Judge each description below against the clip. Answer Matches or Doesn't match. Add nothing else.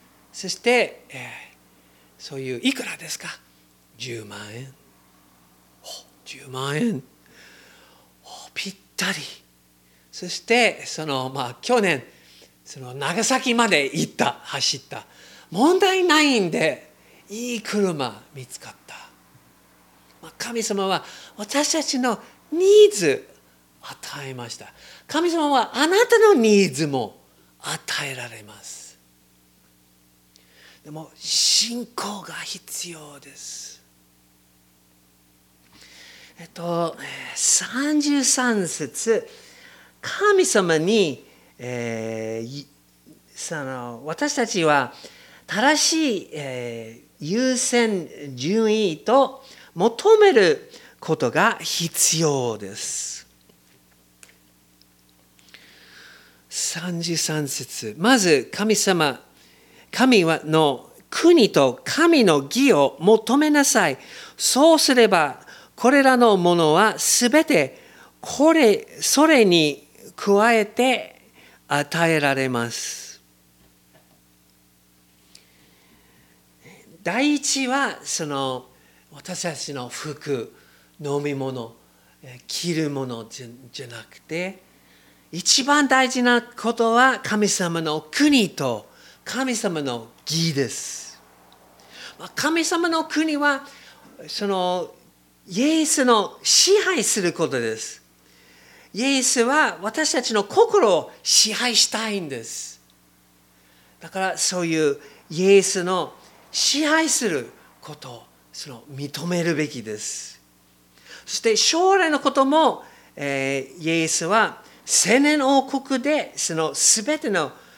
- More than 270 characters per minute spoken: Doesn't match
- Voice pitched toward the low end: Doesn't match